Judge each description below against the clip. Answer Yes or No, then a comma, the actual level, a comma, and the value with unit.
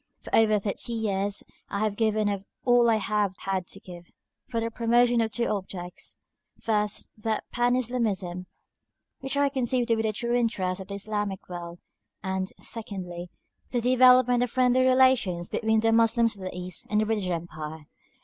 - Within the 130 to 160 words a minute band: No, average, 175 wpm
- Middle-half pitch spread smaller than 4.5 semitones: Yes, average, 4.0 semitones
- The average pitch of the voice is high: Yes, high, 215 Hz